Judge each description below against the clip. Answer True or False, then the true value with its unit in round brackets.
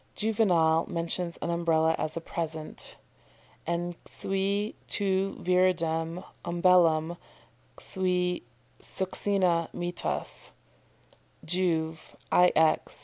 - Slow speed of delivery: True (85 wpm)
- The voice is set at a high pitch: False (175 Hz)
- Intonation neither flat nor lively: False (2.2 semitones)